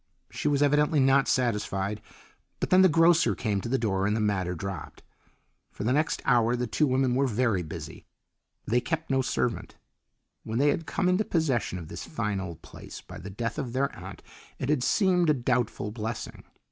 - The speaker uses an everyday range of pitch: No, wide, 5.7 semitones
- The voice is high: No, low, 125 Hz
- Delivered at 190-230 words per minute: Yes, average, 195 wpm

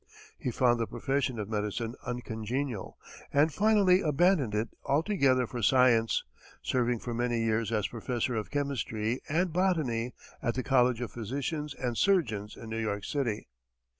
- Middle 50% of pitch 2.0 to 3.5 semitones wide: No, average, 3.9 semitones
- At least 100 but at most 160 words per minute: Yes, average, 150 wpm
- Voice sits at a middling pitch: No, low, 125 Hz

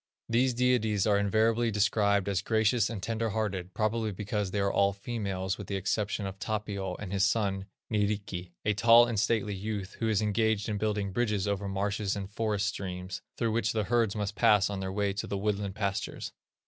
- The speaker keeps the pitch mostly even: Yes, narrow, 1.9 semitones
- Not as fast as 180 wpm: No, average, 195 wpm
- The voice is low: Yes, low, 105 Hz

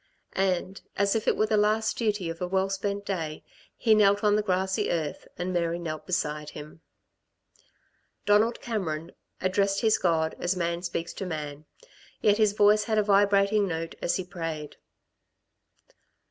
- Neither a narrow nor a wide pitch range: Yes, average, 3.7 semitones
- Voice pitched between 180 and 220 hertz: Yes, high, 190 Hz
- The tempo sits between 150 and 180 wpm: Yes, average, 160 wpm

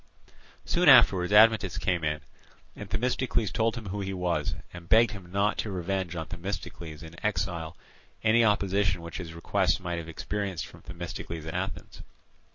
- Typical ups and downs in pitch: Yes, average, 3.6 semitones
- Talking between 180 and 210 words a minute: No, average, 165 wpm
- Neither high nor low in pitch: No, very low, 95 Hz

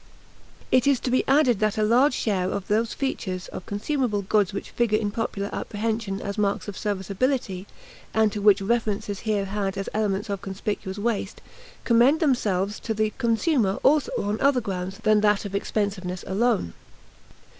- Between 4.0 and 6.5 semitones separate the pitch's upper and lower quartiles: No, average, 2.8 semitones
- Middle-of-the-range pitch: No, high, 210 Hz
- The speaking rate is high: No, average, 170 wpm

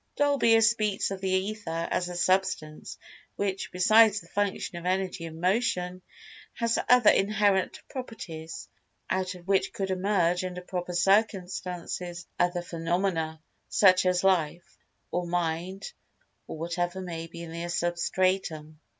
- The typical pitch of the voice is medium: Yes, medium, 180 Hz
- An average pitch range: No, narrow, 2.2 semitones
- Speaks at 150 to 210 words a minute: No, slow, 135 wpm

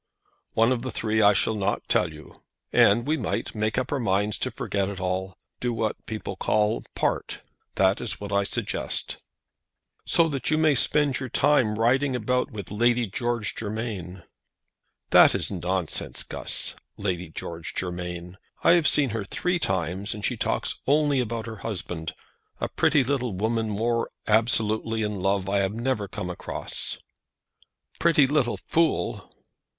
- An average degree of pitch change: Yes, average, 4.4 semitones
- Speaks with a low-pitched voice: Yes, low, 110 Hz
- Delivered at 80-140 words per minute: No, average, 160 wpm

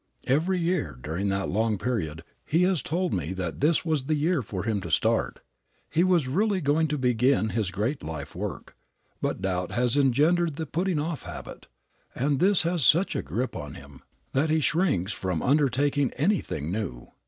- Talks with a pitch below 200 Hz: Yes, low, 135 Hz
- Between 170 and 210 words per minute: Yes, average, 180 wpm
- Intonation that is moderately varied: No, wide, 8.8 semitones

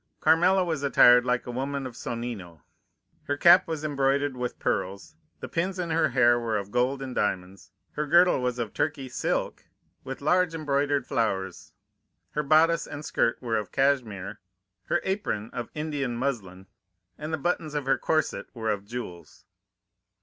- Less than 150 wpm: No, average, 165 wpm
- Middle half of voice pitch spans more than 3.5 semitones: Yes, average, 5.0 semitones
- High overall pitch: No, low, 135 Hz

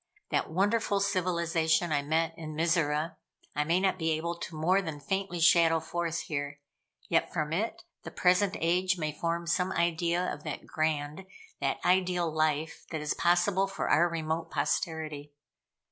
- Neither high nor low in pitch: Yes, medium, 170 Hz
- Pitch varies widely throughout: No, narrow, 2.5 semitones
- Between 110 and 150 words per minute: No, average, 160 wpm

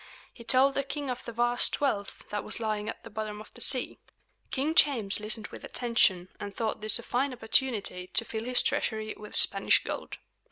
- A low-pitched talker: No, high, 225 Hz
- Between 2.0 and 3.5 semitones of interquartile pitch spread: Yes, average, 3.0 semitones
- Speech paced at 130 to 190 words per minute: No, average, 200 wpm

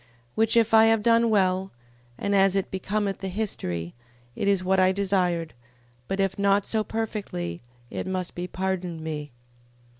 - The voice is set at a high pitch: Yes, high, 195 Hz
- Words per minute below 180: Yes, average, 170 wpm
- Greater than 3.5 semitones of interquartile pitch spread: No, narrow, 2.4 semitones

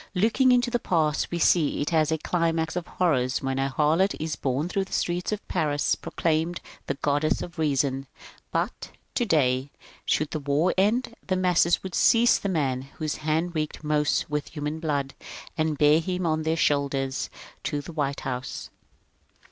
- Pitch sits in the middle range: Yes, medium, 155 Hz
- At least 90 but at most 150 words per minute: No, average, 170 wpm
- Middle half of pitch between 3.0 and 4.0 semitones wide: Yes, average, 3.4 semitones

